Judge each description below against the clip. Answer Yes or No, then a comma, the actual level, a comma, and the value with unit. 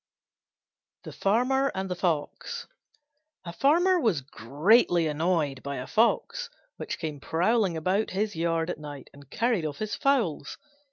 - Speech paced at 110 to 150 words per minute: Yes, average, 145 wpm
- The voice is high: No, medium, 175 Hz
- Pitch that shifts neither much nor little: No, wide, 6.8 semitones